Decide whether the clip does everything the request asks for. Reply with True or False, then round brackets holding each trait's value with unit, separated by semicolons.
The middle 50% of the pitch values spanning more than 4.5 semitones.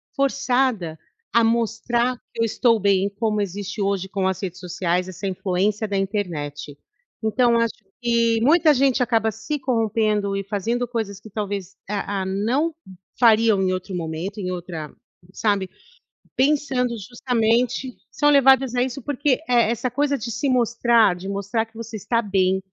False (3.9 semitones)